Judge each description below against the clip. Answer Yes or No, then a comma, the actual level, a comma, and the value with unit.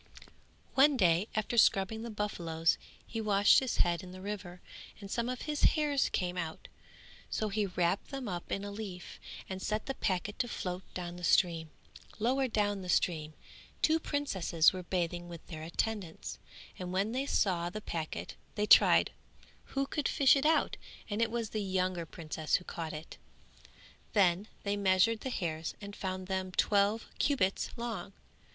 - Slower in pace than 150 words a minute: No, average, 170 wpm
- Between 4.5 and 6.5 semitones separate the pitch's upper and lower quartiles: No, average, 4.0 semitones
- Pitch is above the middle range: Yes, high, 195 Hz